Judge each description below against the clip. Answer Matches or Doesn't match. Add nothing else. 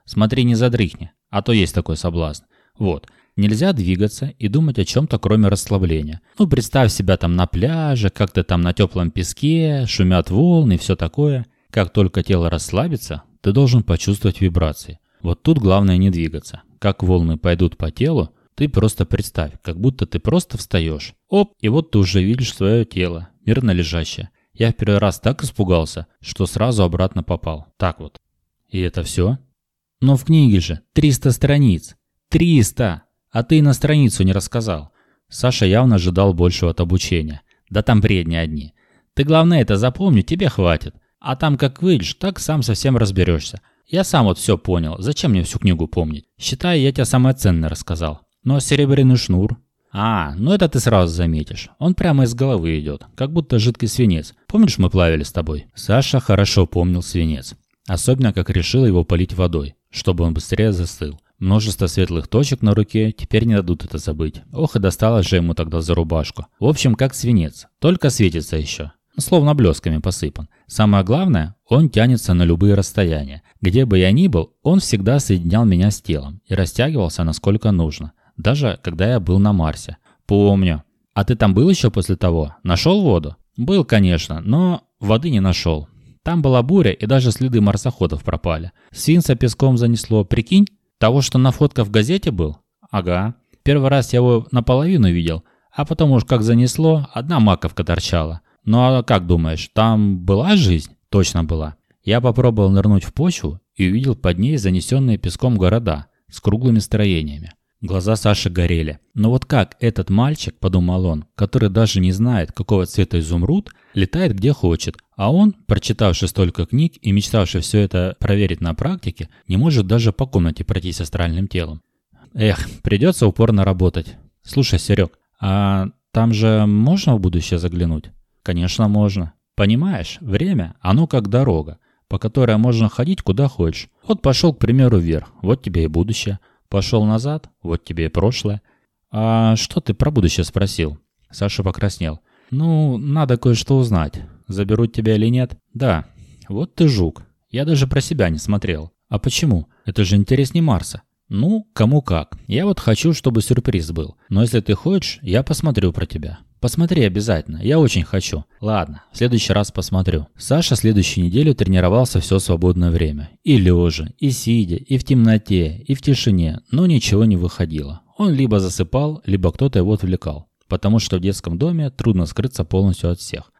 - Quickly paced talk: Matches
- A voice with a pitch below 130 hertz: Matches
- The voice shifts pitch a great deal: Matches